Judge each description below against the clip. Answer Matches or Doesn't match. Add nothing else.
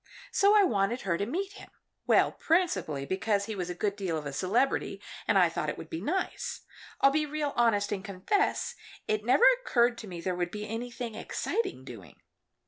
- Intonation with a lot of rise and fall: Matches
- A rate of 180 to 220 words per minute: Matches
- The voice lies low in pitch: Doesn't match